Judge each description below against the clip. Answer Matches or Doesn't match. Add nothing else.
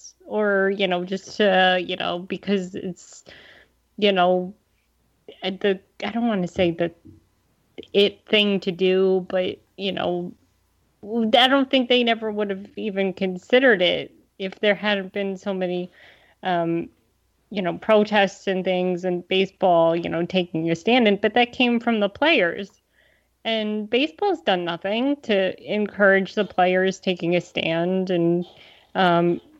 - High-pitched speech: Matches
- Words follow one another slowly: Doesn't match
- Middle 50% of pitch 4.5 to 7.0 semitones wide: Doesn't match